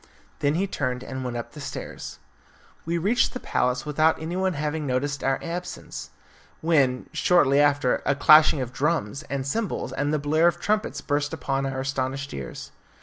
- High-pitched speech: No, medium, 145 Hz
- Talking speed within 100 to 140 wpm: No, average, 170 wpm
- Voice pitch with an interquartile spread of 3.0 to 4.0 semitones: Yes, average, 3.3 semitones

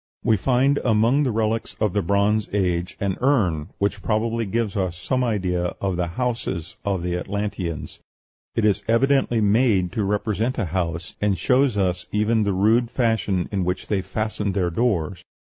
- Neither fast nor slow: Yes, average, 170 wpm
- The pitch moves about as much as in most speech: Yes, average, 3.8 semitones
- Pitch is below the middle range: Yes, low, 105 Hz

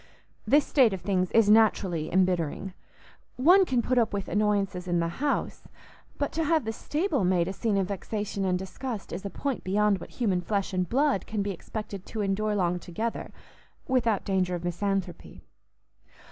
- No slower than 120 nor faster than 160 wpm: No, average, 175 wpm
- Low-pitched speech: No, high, 200 Hz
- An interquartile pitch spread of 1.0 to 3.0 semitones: No, average, 3.8 semitones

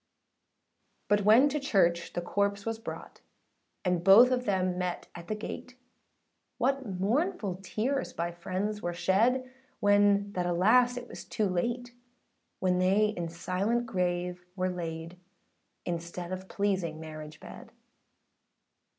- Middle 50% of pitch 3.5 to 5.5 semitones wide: Yes, average, 3.9 semitones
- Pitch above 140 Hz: Yes, high, 190 Hz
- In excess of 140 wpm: No, slow, 135 wpm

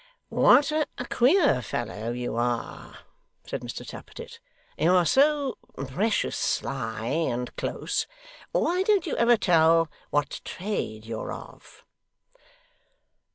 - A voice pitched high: No, medium, 165 Hz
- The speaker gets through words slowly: Yes, slow, 110 wpm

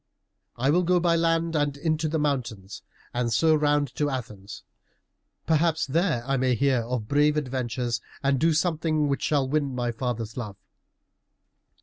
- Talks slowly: No, average, 155 wpm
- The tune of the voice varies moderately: Yes, average, 4.2 semitones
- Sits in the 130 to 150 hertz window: Yes, medium, 140 Hz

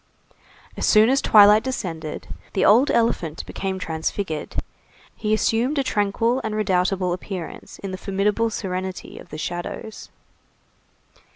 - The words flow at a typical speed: No, slow, 125 wpm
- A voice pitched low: No, high, 200 Hz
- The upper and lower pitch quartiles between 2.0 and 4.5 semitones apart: Yes, average, 3.3 semitones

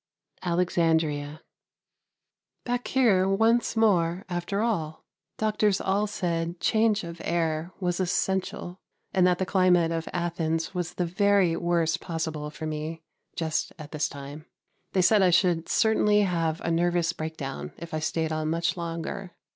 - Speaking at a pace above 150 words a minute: No, average, 145 wpm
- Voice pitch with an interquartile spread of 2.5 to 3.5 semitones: Yes, average, 2.8 semitones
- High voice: No, medium, 170 Hz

